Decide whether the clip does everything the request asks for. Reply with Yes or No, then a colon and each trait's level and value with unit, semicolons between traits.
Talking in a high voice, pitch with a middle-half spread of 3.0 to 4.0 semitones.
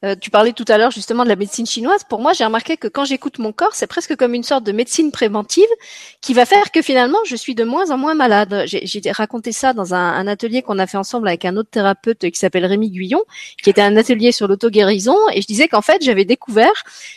No: high, 230 Hz; average, 4.9 semitones